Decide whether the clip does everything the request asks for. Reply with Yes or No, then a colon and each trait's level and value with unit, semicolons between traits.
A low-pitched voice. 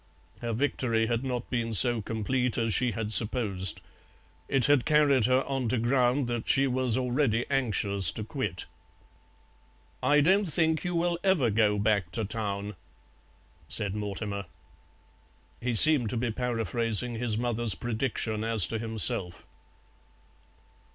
Yes: low, 115 Hz